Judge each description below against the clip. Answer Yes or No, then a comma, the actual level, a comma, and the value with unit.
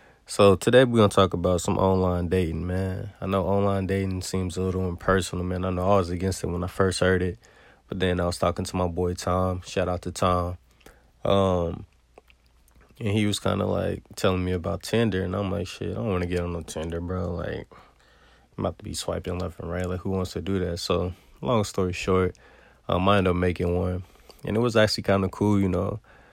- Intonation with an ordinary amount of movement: No, narrow, 1.8 semitones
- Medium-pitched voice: No, very low, 90 Hz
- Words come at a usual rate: No, fast, 230 wpm